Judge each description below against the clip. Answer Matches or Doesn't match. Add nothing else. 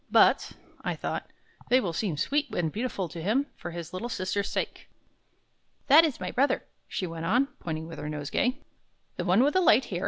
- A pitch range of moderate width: Doesn't match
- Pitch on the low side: Doesn't match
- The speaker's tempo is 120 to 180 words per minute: Doesn't match